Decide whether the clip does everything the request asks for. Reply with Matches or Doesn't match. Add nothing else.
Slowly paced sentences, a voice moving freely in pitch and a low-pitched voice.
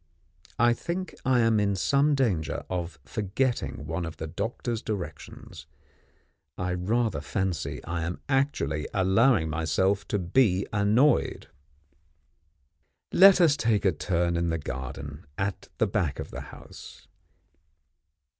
Matches